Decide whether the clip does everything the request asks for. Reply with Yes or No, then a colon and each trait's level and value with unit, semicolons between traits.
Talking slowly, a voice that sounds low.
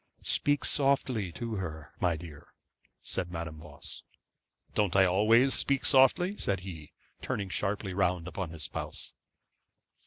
Yes: slow, 130 wpm; very low, 95 Hz